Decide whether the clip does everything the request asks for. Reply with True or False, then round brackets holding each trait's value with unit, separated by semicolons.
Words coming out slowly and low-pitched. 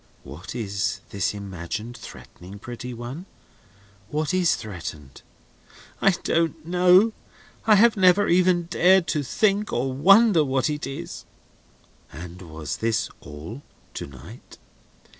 True (120 wpm; 130 Hz)